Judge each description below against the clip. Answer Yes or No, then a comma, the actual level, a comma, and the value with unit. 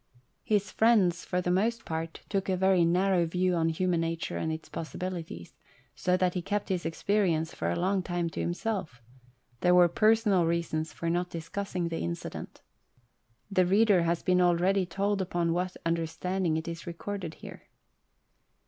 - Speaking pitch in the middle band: Yes, medium, 180 Hz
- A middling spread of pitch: No, narrow, 2.3 semitones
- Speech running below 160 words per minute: No, average, 165 wpm